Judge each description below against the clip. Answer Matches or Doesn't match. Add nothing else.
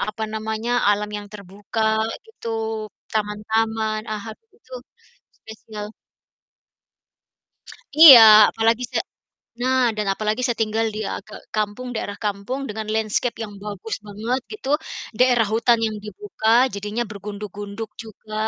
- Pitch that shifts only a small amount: Matches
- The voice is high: Matches